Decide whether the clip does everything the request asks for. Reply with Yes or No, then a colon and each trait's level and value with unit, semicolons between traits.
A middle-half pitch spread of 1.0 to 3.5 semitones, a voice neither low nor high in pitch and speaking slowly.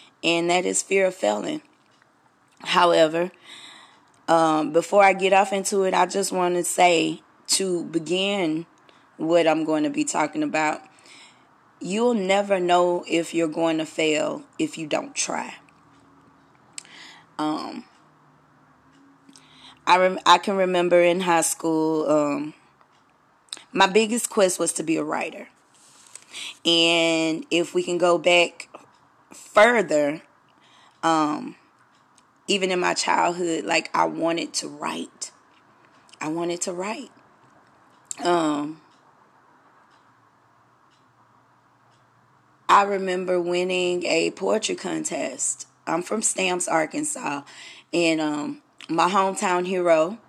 Yes: average, 3.0 semitones; medium, 175 Hz; slow, 115 wpm